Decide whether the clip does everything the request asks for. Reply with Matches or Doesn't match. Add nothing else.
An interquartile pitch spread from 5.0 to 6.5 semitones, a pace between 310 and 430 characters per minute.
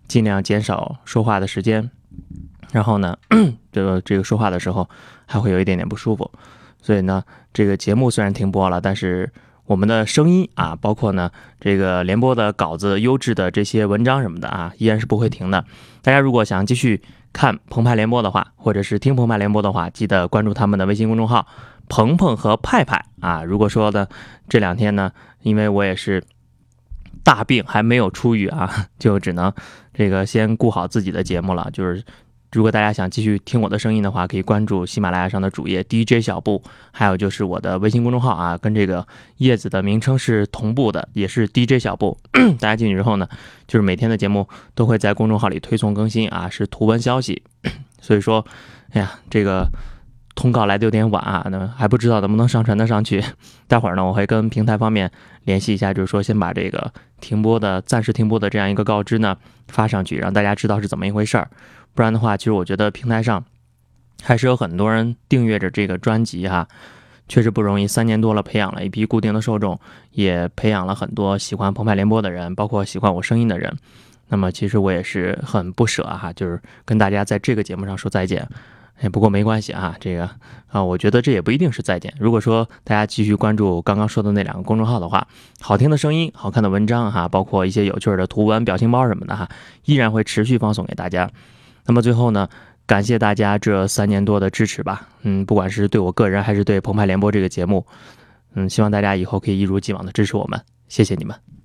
Doesn't match